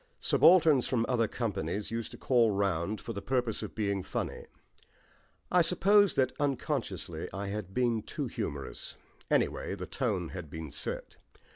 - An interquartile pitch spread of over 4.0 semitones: Yes, average, 5.0 semitones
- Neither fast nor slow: Yes, average, 150 wpm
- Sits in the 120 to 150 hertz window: No, low, 110 Hz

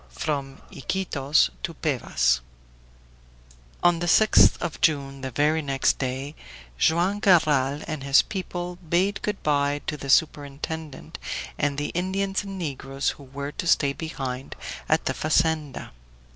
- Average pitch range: Yes, average, 4.0 semitones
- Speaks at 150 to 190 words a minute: No, slow, 135 wpm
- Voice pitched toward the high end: No, medium, 150 Hz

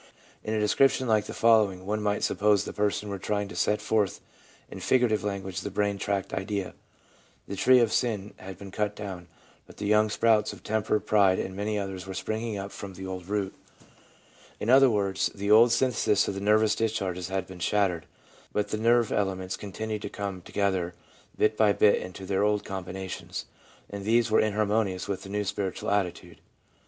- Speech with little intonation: Yes, narrow, 2.0 semitones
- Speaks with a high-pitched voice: No, low, 100 Hz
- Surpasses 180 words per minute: Yes, average, 190 wpm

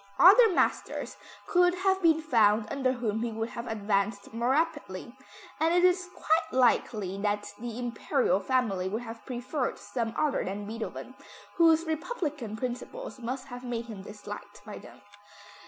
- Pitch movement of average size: No, wide, 6.6 semitones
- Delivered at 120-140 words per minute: No, average, 155 wpm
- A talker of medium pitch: No, high, 245 Hz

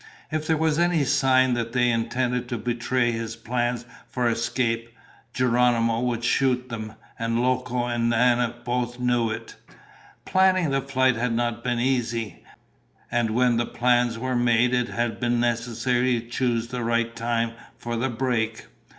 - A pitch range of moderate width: No, narrow, 1.3 semitones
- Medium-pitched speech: No, low, 120 Hz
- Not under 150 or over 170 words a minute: Yes, average, 160 wpm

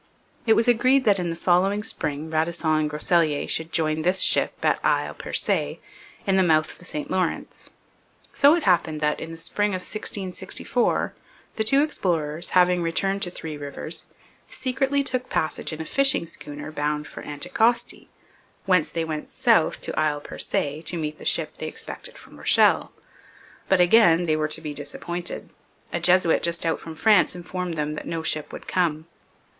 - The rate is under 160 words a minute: No, average, 175 wpm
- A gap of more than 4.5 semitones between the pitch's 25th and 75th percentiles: No, average, 3.8 semitones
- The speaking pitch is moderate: Yes, medium, 170 Hz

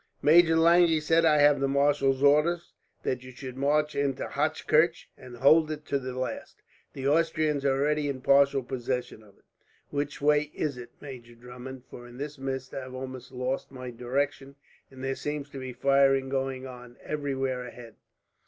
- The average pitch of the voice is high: No, low, 135 Hz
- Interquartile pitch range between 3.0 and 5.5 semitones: No, narrow, 2.4 semitones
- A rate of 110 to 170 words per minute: No, average, 180 wpm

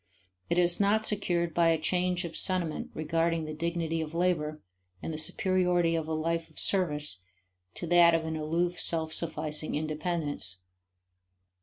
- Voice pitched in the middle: Yes, medium, 165 Hz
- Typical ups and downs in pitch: No, narrow, 2.0 semitones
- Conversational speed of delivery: Yes, average, 155 wpm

